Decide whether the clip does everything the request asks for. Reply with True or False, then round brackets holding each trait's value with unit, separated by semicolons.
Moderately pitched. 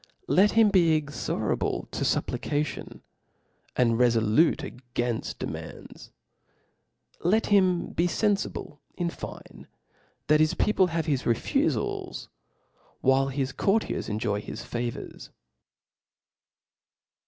True (150 Hz)